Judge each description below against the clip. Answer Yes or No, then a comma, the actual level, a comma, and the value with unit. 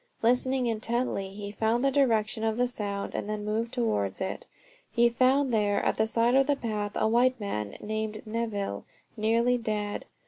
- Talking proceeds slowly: No, average, 175 wpm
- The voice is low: No, high, 220 Hz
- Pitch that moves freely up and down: No, average, 2.7 semitones